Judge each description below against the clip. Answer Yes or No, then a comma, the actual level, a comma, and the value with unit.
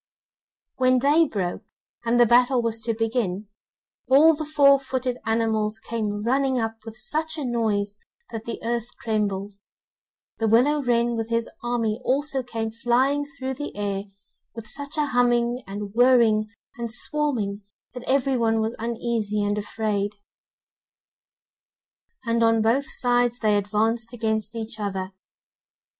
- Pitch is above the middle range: Yes, high, 230 Hz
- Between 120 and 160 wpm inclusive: Yes, average, 140 wpm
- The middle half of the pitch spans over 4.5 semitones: No, average, 2.8 semitones